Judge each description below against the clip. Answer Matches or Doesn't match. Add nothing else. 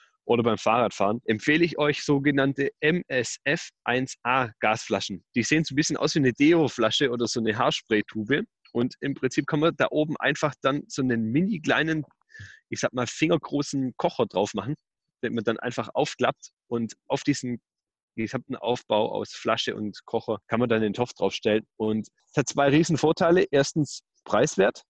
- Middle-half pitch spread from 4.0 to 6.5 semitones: Matches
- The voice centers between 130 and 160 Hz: Matches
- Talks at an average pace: Matches